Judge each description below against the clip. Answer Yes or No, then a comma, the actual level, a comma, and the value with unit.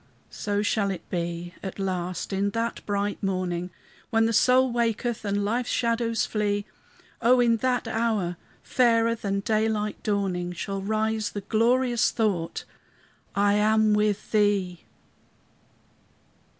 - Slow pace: Yes, slow, 125 wpm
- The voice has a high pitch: Yes, high, 210 Hz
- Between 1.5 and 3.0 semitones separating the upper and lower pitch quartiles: Yes, narrow, 2.6 semitones